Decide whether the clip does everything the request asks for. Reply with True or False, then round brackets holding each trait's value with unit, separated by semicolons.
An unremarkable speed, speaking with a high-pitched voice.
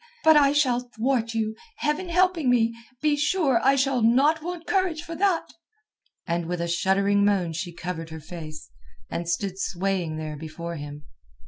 True (165 wpm; 220 Hz)